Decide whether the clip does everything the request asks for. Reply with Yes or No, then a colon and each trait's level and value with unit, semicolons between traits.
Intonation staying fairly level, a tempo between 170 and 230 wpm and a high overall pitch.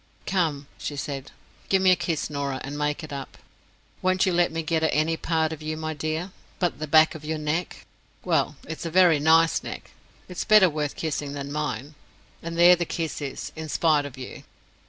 No: narrow, 2.3 semitones; average, 200 wpm; medium, 155 Hz